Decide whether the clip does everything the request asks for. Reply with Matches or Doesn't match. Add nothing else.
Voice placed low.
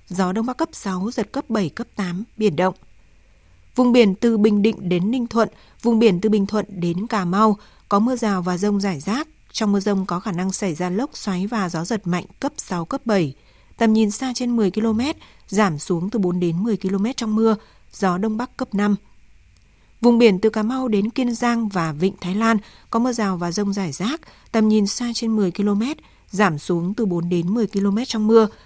Doesn't match